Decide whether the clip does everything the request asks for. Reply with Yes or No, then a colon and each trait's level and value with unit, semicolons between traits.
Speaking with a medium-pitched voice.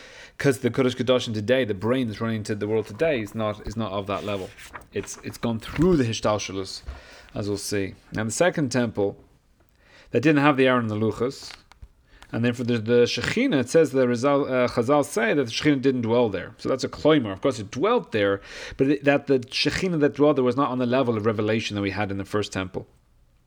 No: low, 120 Hz